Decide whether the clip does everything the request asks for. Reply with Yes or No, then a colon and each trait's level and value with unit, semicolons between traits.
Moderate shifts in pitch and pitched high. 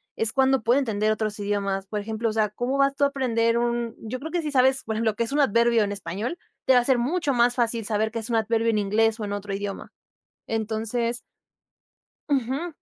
Yes: average, 3.0 semitones; high, 230 Hz